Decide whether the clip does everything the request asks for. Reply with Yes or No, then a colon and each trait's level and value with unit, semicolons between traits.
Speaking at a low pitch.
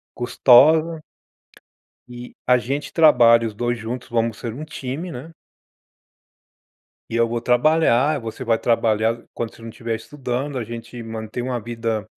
Yes: low, 120 Hz